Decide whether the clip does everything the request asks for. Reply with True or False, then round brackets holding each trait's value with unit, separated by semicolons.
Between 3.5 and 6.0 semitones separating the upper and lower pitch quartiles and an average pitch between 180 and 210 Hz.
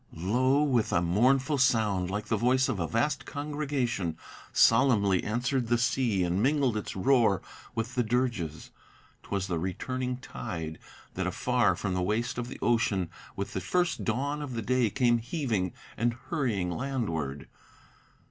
False (5.2 semitones; 115 Hz)